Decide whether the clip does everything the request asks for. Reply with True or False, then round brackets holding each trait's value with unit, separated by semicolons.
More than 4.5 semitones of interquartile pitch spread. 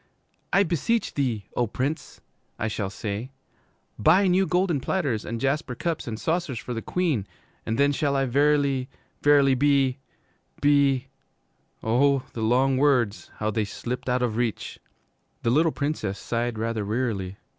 False (4.1 semitones)